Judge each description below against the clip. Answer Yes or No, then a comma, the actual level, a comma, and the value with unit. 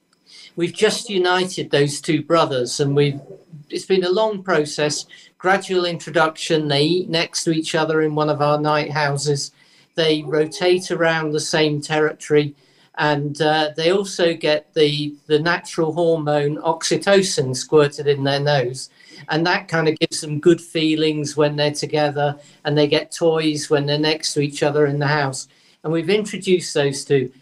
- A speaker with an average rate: Yes, average, 165 wpm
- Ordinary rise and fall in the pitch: No, narrow, 2.2 semitones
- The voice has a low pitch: No, medium, 155 Hz